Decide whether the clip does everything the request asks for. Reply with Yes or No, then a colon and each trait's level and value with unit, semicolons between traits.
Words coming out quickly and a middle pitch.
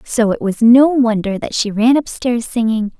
No: fast, 220 wpm; high, 235 Hz